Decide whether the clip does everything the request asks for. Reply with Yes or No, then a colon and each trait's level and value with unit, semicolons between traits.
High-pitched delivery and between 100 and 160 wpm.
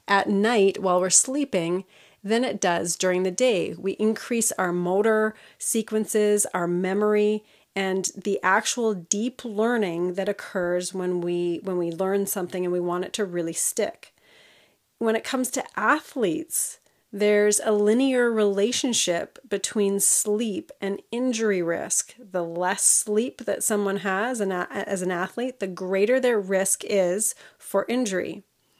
Yes: high, 200 Hz; average, 140 wpm